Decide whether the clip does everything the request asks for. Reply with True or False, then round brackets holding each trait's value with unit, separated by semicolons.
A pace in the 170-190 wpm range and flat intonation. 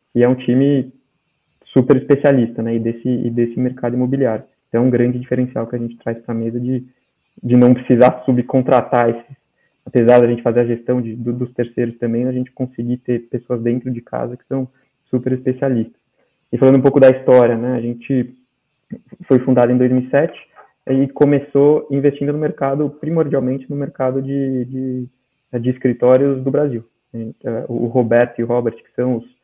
True (180 wpm; 1.8 semitones)